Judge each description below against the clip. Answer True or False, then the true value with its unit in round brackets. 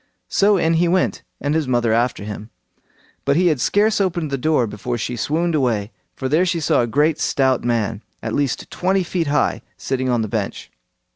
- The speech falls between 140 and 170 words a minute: False (200 wpm)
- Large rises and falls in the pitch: True (5.9 semitones)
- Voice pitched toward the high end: False (140 Hz)